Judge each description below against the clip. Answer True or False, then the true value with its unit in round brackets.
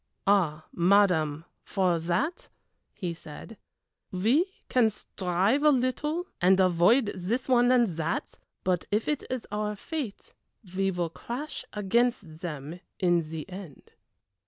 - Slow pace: True (130 wpm)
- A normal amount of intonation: False (5.8 semitones)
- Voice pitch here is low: False (195 Hz)